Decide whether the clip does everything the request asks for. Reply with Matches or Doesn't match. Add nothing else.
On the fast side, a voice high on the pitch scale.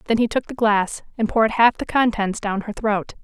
Matches